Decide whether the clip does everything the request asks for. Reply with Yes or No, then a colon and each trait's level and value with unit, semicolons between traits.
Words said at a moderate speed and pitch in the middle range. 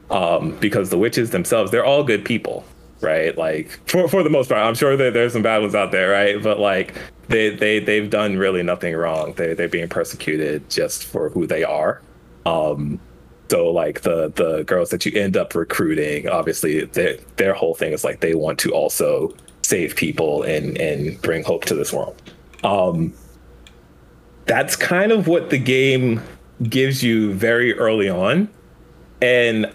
No: average, 180 wpm; low, 115 Hz